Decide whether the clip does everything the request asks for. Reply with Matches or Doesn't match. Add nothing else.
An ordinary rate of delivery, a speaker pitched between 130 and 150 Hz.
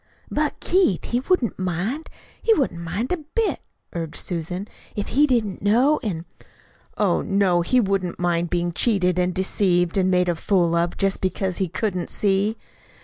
Doesn't match